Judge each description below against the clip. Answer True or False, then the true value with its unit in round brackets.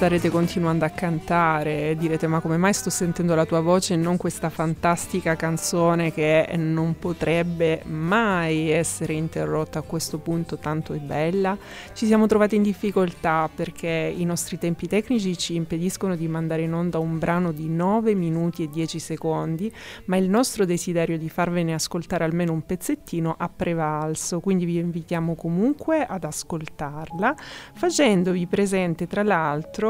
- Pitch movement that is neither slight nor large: False (2.3 semitones)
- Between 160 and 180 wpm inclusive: False (150 wpm)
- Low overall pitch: False (170 Hz)